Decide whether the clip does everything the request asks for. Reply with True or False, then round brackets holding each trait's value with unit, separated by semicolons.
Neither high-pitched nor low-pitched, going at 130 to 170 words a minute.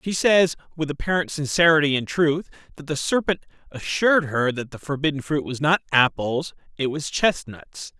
True (150 Hz; 165 wpm)